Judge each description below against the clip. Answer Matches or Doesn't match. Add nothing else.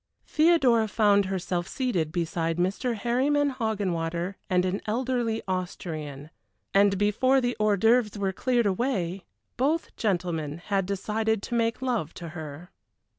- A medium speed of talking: Doesn't match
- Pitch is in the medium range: Doesn't match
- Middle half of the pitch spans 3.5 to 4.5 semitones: Doesn't match